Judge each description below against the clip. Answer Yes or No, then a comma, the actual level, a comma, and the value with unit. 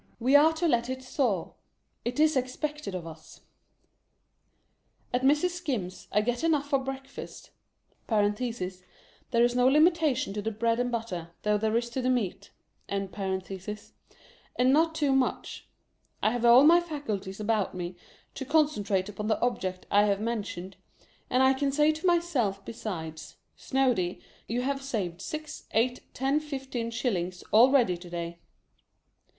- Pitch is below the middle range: No, high, 235 Hz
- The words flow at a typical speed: Yes, average, 145 wpm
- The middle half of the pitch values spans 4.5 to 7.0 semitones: Yes, wide, 5.5 semitones